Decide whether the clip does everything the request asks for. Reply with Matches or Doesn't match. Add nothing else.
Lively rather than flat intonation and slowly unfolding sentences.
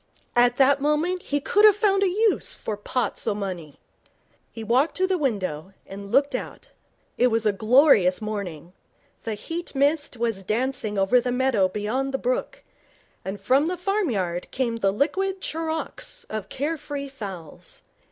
Doesn't match